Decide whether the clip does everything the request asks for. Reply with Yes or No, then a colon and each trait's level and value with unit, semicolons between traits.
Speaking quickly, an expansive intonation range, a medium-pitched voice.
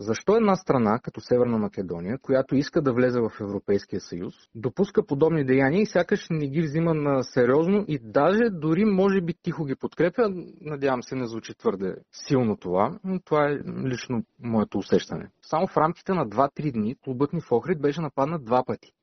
Yes: fast, 185 wpm; wide, 5.9 semitones; medium, 150 Hz